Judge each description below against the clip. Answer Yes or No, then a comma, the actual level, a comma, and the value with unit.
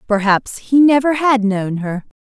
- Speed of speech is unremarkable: Yes, average, 160 wpm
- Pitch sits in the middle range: No, high, 230 Hz